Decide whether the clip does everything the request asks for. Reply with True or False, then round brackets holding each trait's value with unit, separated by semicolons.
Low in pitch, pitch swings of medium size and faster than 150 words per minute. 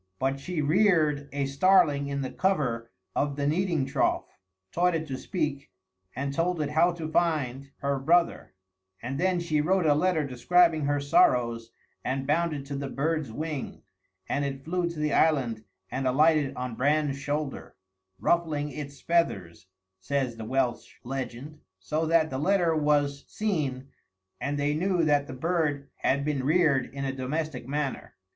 False (145 Hz; 3.1 semitones; 165 wpm)